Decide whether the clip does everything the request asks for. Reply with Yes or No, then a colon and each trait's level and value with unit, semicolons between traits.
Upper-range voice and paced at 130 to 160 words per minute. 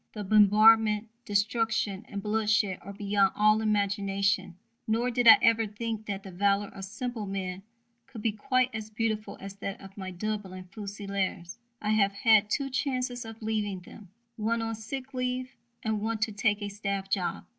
No: high, 210 Hz; average, 170 wpm